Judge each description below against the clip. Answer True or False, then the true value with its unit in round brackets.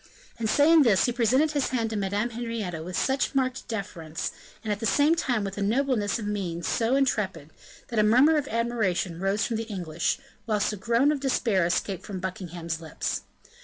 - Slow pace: False (195 wpm)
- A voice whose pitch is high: True (220 Hz)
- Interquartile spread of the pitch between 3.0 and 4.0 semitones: False (4.8 semitones)